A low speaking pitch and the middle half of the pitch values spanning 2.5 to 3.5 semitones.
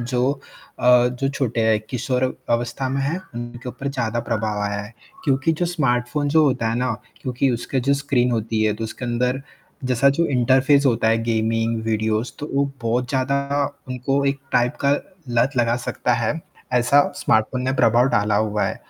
Yes: low, 125 Hz; average, 3.0 semitones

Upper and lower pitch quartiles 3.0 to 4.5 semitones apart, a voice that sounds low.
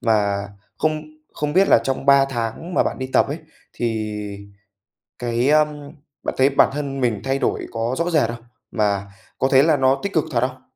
Yes: average, 4.2 semitones; low, 130 Hz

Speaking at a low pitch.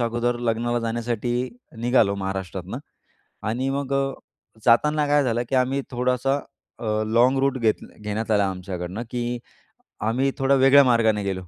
Yes: low, 120 Hz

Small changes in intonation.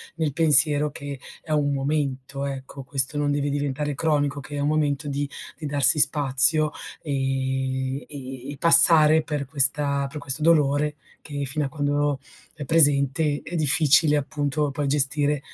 Yes: narrow, 1.6 semitones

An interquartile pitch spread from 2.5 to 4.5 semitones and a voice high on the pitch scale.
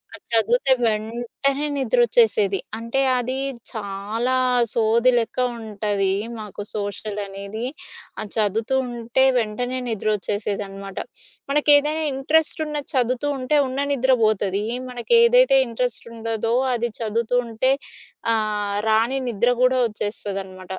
Yes: average, 3.4 semitones; high, 225 Hz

